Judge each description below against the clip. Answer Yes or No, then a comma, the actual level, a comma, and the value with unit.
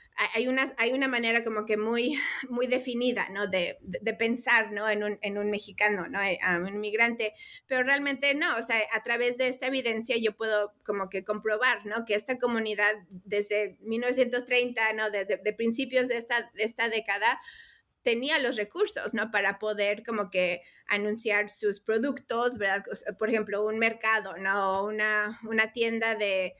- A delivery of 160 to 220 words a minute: Yes, average, 175 wpm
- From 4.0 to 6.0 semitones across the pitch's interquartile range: No, average, 2.8 semitones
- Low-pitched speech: No, high, 220 Hz